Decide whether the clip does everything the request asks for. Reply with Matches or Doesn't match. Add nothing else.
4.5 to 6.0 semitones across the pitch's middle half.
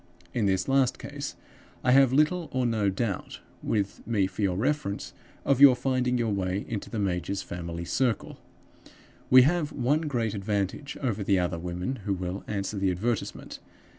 Matches